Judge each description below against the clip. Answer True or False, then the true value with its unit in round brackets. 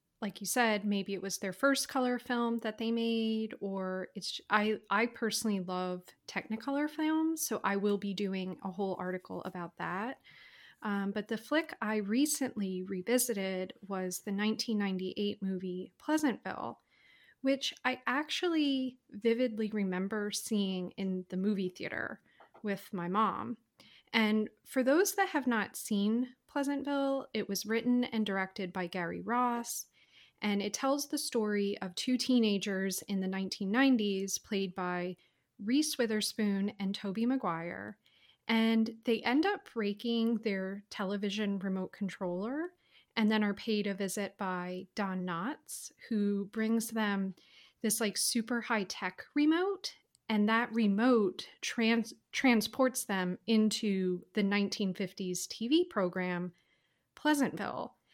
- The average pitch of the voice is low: False (215 Hz)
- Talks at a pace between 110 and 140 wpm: True (135 wpm)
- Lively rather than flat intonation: False (3.9 semitones)